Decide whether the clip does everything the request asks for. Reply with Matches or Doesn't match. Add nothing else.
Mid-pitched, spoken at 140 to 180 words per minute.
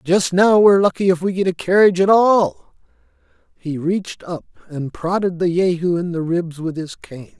Doesn't match